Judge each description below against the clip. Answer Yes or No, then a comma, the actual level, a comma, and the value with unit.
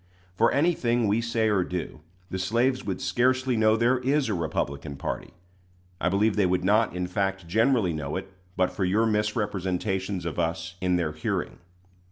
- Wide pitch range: No, average, 4.1 semitones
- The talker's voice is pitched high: No, low, 100 Hz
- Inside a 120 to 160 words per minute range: No, average, 175 wpm